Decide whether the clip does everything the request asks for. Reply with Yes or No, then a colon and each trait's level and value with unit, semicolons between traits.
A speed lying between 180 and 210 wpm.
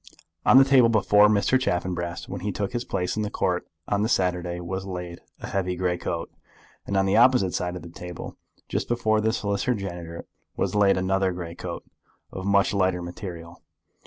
Yes: average, 190 wpm